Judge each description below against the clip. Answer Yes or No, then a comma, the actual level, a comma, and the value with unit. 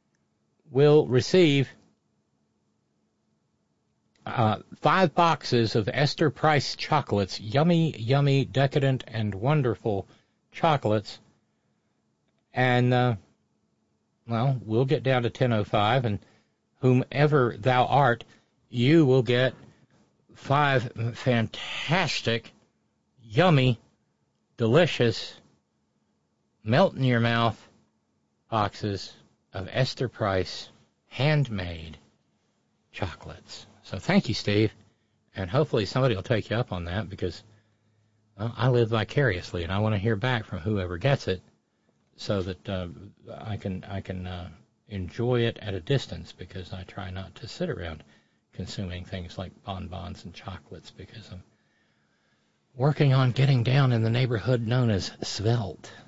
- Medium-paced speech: No, slow, 115 wpm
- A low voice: Yes, low, 115 Hz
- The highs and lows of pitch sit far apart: No, average, 5.0 semitones